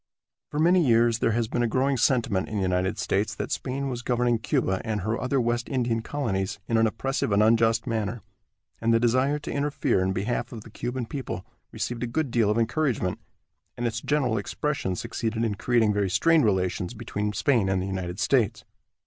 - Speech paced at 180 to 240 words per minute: Yes, average, 200 wpm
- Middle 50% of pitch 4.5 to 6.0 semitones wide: No, average, 3.4 semitones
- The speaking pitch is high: No, low, 115 Hz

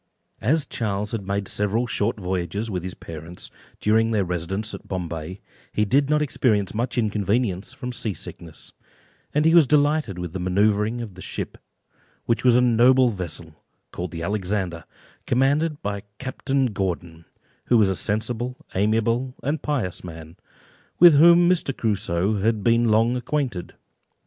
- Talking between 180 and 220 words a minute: No, average, 155 wpm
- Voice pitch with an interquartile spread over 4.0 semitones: Yes, average, 5.2 semitones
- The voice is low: Yes, low, 110 Hz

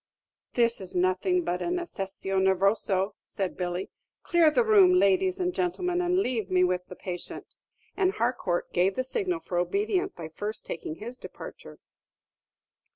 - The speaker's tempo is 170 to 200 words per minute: No, average, 155 wpm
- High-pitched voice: Yes, high, 225 Hz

